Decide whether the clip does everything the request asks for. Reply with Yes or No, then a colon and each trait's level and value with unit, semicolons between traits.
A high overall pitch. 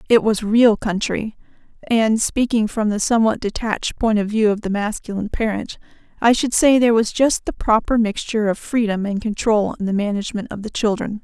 Yes: high, 215 Hz